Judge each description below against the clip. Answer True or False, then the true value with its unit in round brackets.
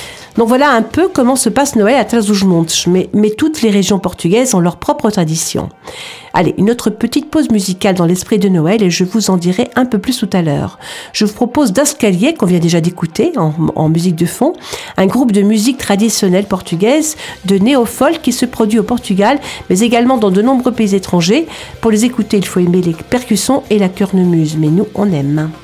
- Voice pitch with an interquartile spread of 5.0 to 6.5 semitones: True (5.3 semitones)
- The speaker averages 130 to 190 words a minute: False (210 wpm)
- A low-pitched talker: False (210 Hz)